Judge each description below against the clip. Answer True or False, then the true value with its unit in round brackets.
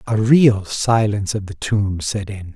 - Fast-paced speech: False (190 wpm)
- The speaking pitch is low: True (105 Hz)